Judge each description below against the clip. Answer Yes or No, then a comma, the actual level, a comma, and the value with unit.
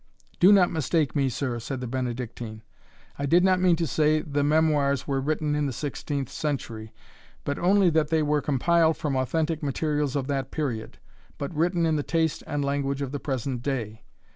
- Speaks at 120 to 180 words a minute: No, average, 190 wpm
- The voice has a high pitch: No, medium, 145 Hz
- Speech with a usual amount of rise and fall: Yes, average, 3.1 semitones